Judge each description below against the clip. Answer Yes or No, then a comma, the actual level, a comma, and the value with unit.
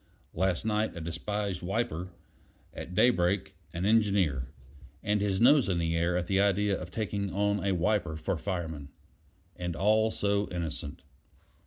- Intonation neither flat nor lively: Yes, average, 3.1 semitones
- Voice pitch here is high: No, very low, 95 Hz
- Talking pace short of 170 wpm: Yes, average, 150 wpm